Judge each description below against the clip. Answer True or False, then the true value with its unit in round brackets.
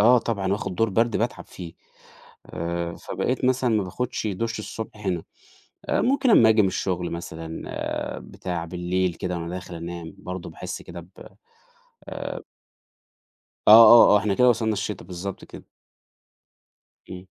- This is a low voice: True (95 Hz)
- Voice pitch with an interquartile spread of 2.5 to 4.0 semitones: False (4.4 semitones)